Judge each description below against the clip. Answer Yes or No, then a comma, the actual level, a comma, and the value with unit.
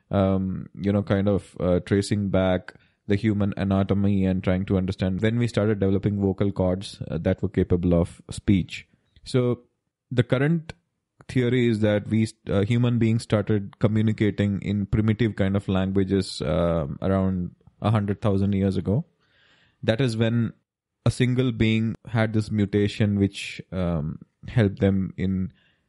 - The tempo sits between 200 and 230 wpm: No, average, 155 wpm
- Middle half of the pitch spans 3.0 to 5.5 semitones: No, narrow, 2.6 semitones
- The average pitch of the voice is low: Yes, low, 100 Hz